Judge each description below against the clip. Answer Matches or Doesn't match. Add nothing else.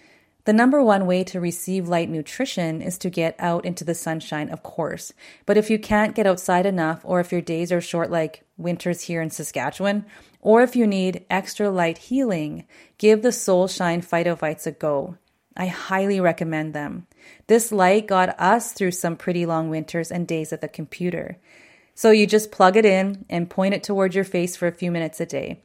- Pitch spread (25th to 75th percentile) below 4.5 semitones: Matches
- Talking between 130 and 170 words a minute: Doesn't match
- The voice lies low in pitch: Doesn't match